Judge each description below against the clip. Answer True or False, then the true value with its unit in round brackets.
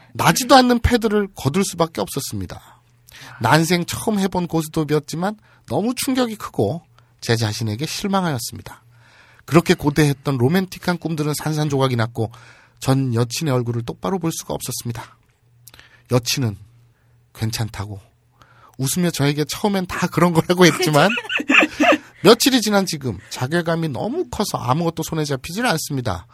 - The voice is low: False (150 Hz)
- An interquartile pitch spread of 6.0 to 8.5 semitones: True (6.9 semitones)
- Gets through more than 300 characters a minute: True (325 characters per minute)